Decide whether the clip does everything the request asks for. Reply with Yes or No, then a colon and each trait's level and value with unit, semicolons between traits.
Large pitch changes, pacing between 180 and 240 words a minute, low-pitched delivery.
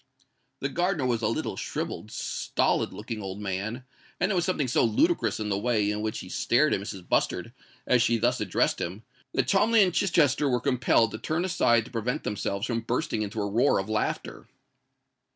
Yes: wide, 5.9 semitones; average, 195 wpm; low, 120 Hz